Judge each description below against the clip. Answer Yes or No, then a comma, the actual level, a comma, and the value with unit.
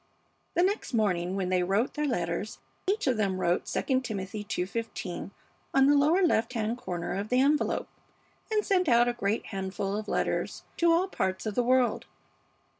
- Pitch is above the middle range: Yes, high, 230 Hz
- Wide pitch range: Yes, wide, 6.2 semitones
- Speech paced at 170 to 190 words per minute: Yes, average, 180 wpm